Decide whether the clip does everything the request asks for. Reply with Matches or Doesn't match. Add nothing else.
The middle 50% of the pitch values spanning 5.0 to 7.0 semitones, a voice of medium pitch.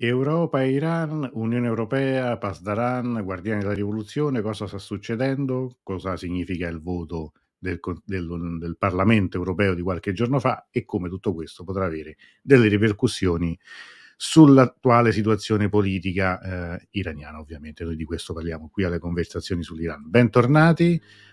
Doesn't match